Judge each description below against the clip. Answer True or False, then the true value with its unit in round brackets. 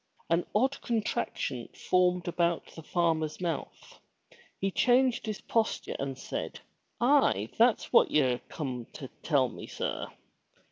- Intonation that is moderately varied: False (7.3 semitones)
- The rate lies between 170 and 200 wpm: False (135 wpm)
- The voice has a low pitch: False (175 Hz)